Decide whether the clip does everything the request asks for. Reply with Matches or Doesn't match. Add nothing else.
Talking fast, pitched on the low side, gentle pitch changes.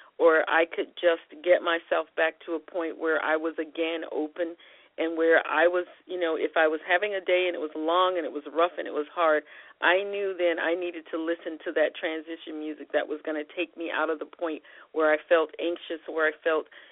Doesn't match